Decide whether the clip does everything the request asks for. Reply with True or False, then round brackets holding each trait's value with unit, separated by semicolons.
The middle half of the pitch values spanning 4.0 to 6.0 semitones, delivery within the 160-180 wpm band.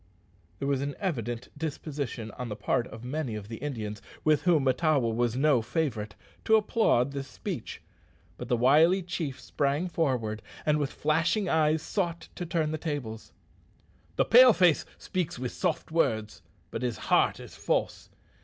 True (5.1 semitones; 165 wpm)